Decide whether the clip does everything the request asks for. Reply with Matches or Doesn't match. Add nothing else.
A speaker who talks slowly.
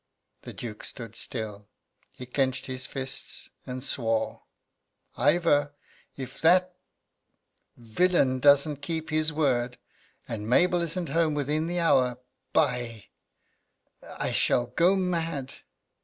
Matches